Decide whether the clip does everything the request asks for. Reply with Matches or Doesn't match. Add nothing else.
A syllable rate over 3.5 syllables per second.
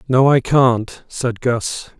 Doesn't match